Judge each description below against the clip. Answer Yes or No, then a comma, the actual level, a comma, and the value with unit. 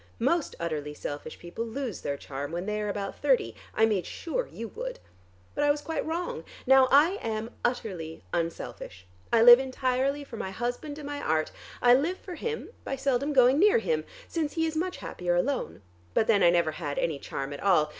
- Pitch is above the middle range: Yes, high, 240 Hz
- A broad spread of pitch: Yes, wide, 8.8 semitones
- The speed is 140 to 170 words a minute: No, average, 200 wpm